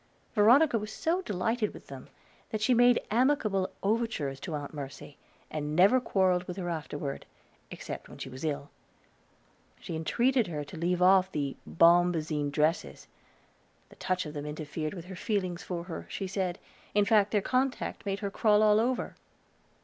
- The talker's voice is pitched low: No, medium, 185 Hz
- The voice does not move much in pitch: No, wide, 5.5 semitones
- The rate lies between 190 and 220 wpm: No, average, 165 wpm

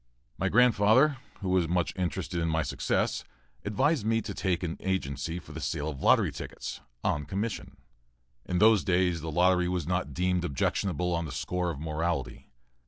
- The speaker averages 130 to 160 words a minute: No, average, 170 wpm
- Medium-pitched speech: No, very low, 90 Hz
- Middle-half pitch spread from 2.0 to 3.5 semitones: Yes, average, 2.7 semitones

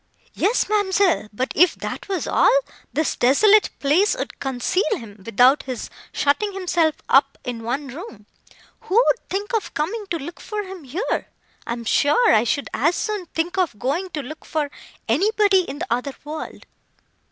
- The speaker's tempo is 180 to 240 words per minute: No, average, 170 wpm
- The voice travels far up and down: Yes, wide, 6.7 semitones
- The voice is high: Yes, very high, 320 Hz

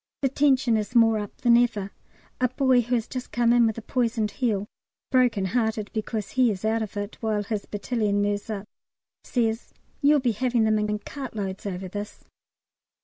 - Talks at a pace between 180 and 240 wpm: Yes, average, 190 wpm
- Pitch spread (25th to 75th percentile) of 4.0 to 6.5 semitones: No, average, 2.9 semitones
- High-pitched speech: Yes, high, 220 Hz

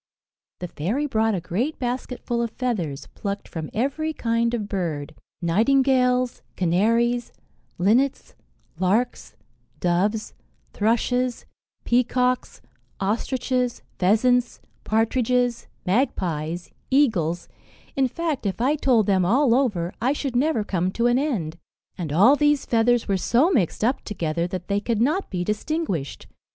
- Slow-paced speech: Yes, slow, 130 wpm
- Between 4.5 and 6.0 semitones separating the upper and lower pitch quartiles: Yes, average, 5.2 semitones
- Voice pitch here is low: No, high, 230 Hz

